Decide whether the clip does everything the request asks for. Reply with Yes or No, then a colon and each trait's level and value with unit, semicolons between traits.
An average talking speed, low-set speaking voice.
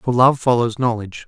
Yes: average, 190 wpm; low, 120 Hz